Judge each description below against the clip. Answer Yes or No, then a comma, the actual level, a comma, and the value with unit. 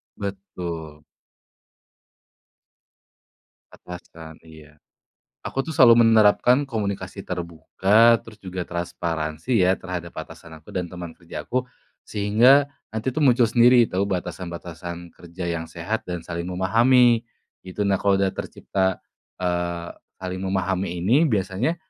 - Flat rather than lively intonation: No, average, 4.5 semitones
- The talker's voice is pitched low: Yes, very low, 95 Hz